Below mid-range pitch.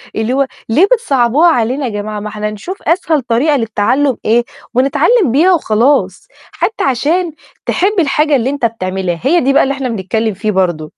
No: very high, 255 Hz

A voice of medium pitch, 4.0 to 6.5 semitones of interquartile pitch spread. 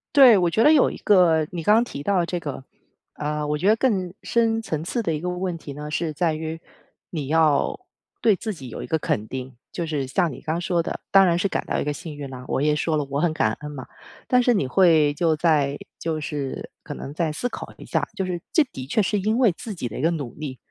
Yes: medium, 165 Hz; average, 4.3 semitones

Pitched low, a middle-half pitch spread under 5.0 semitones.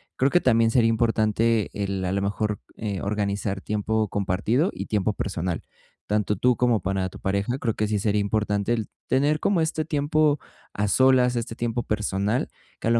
Yes: low, 110 Hz; average, 3.4 semitones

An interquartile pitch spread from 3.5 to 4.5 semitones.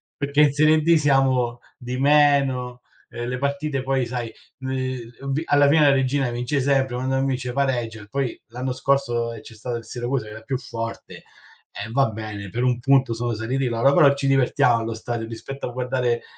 No: narrow, 2.5 semitones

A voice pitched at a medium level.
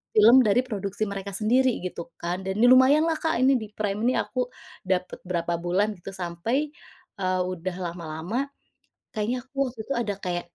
No: high, 200 Hz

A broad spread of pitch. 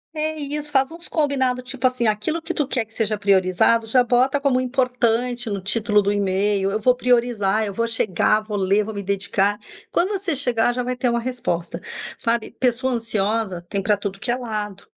No: average, 3.6 semitones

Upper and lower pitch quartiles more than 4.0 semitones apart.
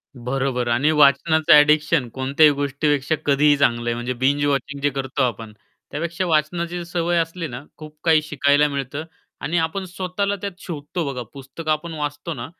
No: average, 3.2 semitones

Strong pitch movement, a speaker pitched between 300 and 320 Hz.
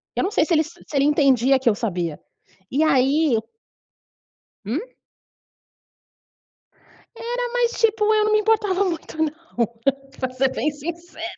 Yes: wide, 6.7 semitones; very high, 315 Hz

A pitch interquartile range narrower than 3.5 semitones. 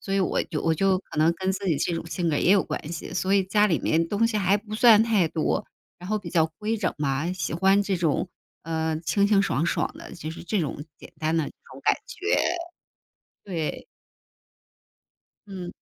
No: average, 3.8 semitones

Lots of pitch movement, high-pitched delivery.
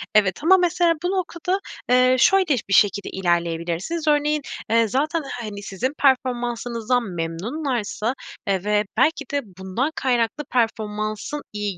Yes: wide, 6.4 semitones; high, 240 Hz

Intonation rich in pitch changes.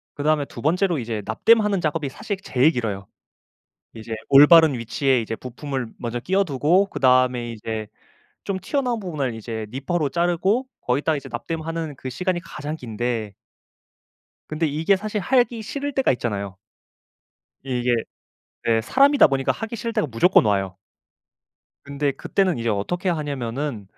Yes: wide, 7.0 semitones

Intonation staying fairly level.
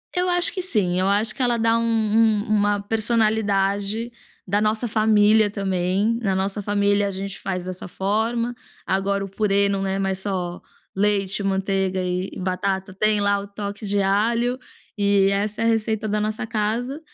Yes: narrow, 2.1 semitones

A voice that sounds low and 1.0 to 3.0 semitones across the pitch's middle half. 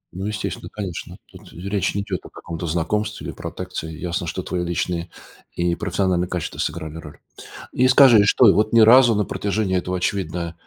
No: very low, 95 Hz; average, 3.5 semitones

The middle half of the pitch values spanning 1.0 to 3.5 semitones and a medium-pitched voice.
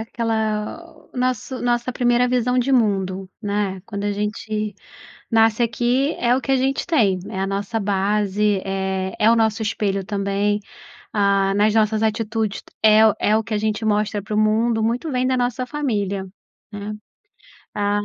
No: average, 2.7 semitones; high, 215 Hz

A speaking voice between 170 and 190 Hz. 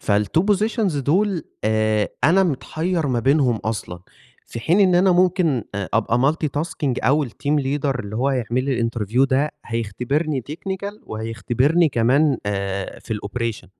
No: low, 135 Hz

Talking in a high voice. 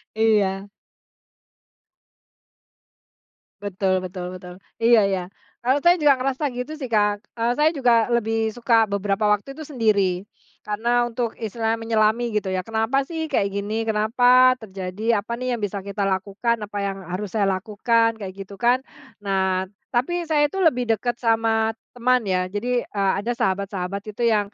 Yes: high, 220 Hz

